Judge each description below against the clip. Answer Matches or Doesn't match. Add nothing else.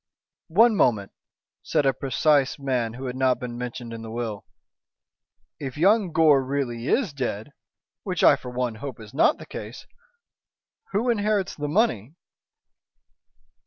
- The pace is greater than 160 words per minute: Doesn't match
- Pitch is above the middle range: Doesn't match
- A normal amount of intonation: Matches